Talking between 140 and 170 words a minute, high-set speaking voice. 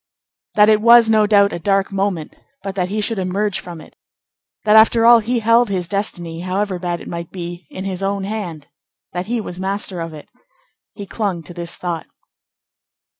No: average, 190 wpm; high, 195 Hz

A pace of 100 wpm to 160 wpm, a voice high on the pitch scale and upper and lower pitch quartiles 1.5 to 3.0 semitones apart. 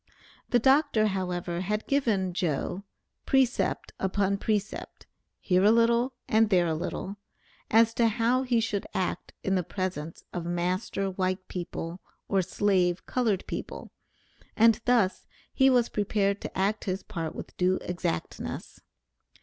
No: average, 140 wpm; high, 195 Hz; average, 3.8 semitones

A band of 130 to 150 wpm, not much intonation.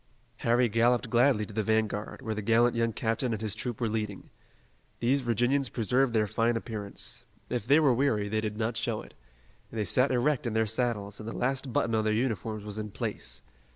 No: fast, 205 wpm; narrow, 2.2 semitones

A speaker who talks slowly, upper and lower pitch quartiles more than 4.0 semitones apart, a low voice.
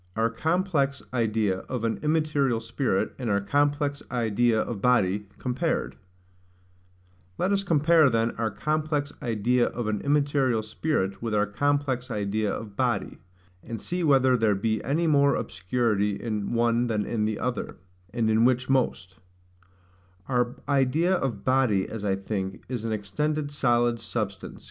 Yes: slow, 120 wpm; average, 4.8 semitones; low, 120 Hz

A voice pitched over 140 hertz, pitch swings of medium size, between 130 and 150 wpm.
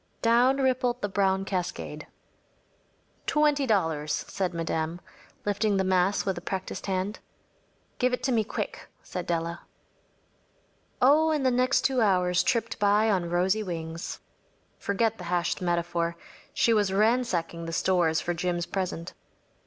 Yes: high, 190 Hz; average, 4.7 semitones; average, 145 wpm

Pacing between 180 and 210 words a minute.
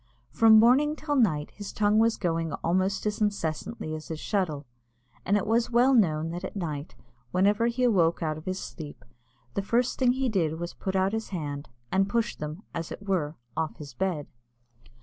Yes: average, 195 wpm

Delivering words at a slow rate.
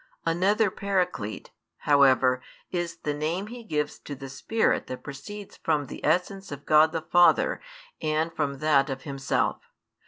No: average, 150 wpm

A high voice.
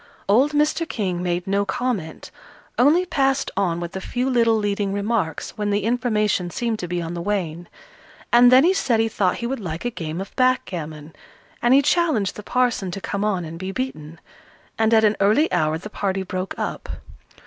Yes: high, 205 Hz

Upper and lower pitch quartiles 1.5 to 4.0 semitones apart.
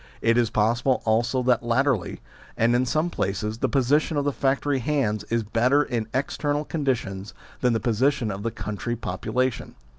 Yes: average, 3.6 semitones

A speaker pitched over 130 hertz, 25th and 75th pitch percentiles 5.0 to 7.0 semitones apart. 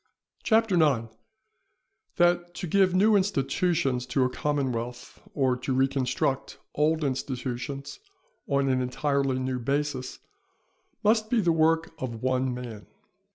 Yes: medium, 140 Hz; wide, 5.4 semitones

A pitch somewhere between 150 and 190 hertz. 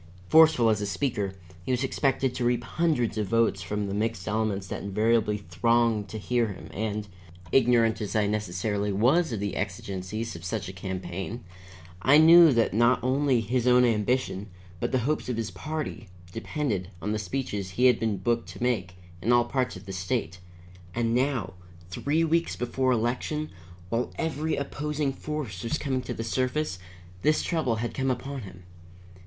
No: low, 115 Hz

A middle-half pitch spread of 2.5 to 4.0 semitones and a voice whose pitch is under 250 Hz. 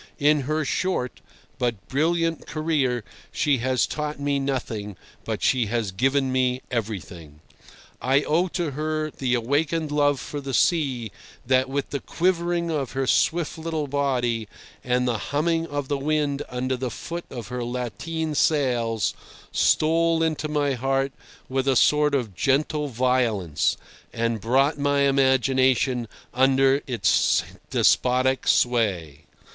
Yes: average, 3.4 semitones; low, 135 Hz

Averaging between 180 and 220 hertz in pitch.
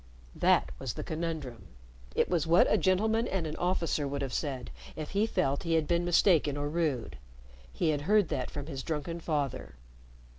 No: medium, 155 Hz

